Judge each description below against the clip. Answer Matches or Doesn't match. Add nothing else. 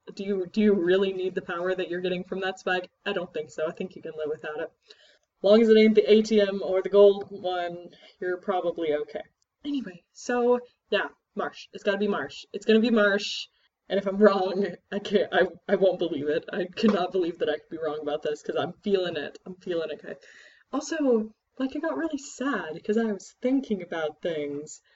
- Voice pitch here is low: Doesn't match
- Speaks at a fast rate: Matches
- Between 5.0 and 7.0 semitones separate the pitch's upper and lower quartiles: Doesn't match